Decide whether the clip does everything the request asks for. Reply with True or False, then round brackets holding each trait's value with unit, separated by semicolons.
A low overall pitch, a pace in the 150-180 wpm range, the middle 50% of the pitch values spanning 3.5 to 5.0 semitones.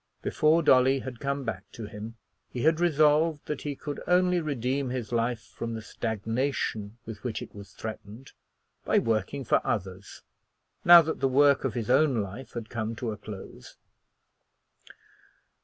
True (125 Hz; 160 wpm; 4.5 semitones)